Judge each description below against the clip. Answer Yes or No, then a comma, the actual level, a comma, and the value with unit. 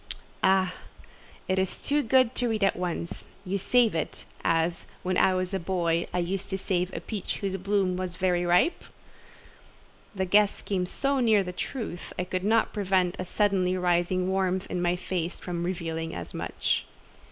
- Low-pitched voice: No, medium, 185 Hz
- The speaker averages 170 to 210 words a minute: Yes, average, 175 wpm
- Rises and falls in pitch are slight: Yes, narrow, 2.0 semitones